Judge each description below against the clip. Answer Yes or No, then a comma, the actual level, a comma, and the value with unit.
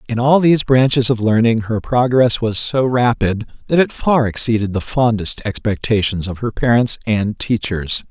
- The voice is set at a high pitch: No, low, 115 Hz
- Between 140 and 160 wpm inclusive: No, average, 170 wpm